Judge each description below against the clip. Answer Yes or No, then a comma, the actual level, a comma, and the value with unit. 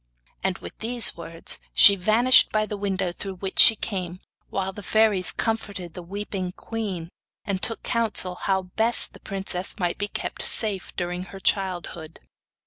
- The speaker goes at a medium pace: Yes, average, 160 wpm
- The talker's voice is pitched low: No, high, 195 Hz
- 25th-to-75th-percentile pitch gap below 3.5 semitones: Yes, average, 2.9 semitones